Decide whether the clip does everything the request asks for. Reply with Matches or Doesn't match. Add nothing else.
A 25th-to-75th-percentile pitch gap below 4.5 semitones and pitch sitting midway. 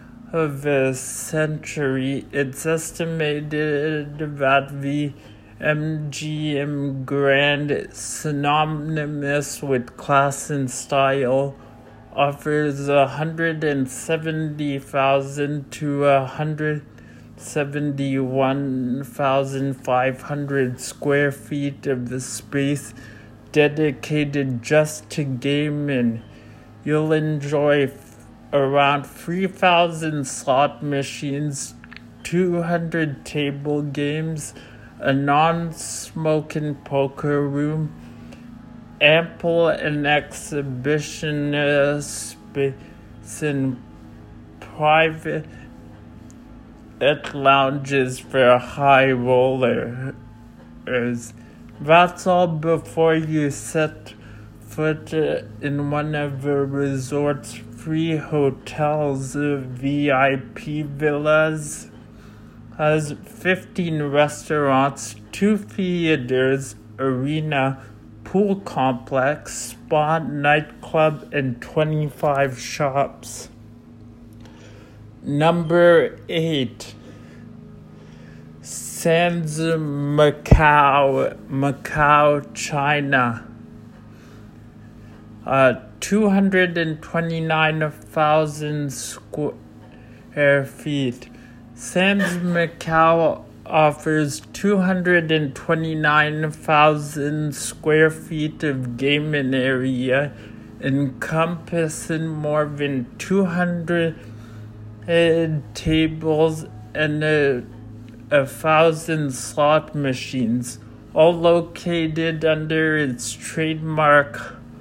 Matches